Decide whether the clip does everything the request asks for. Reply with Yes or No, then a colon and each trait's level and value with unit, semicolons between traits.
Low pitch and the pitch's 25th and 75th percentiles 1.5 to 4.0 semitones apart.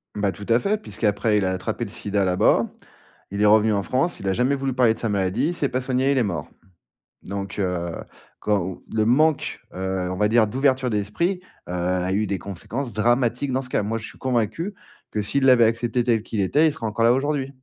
No: low, 110 Hz; average, 4.5 semitones